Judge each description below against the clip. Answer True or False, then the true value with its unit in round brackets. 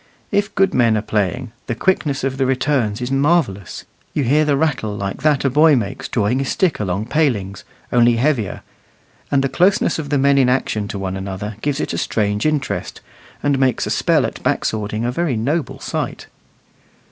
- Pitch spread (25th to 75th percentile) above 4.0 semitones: True (5.3 semitones)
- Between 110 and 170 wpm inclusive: False (195 wpm)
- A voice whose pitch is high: False (130 Hz)